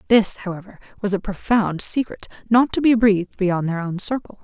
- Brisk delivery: No, average, 190 wpm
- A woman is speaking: Yes, female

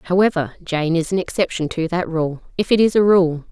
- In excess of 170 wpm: Yes, fast, 205 wpm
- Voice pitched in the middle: Yes, medium, 175 Hz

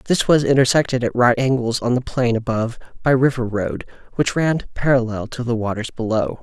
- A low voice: Yes, low, 120 Hz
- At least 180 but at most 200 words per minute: Yes, average, 185 wpm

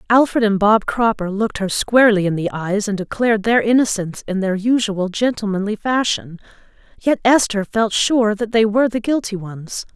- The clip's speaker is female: Yes, female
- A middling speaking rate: Yes, average, 175 wpm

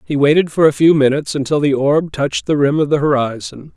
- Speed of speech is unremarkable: No, fast, 240 wpm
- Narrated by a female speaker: No, male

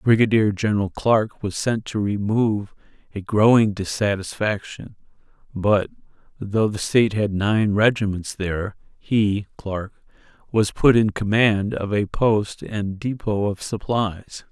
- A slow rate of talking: Yes, slow, 130 wpm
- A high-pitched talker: No, low, 105 Hz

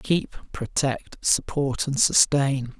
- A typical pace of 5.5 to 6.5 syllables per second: No, 3.2 syllables/s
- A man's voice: Yes, male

